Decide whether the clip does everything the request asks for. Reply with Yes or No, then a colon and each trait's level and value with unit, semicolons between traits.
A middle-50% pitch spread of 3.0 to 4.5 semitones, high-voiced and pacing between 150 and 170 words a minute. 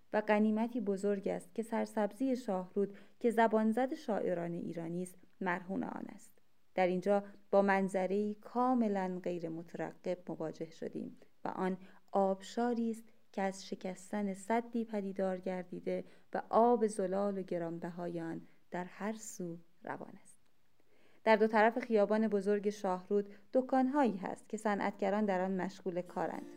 No: average, 3.3 semitones; high, 200 Hz; average, 135 wpm